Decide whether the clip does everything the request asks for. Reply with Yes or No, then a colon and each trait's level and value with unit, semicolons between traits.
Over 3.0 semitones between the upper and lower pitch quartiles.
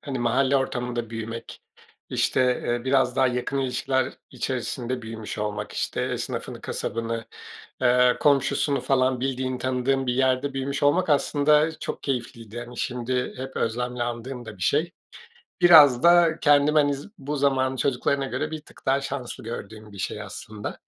No: narrow, 2.6 semitones